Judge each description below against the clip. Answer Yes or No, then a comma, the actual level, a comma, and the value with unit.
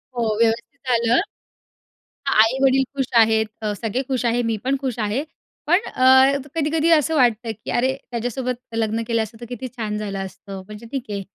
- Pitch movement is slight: No, average, 3.1 semitones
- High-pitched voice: Yes, high, 240 Hz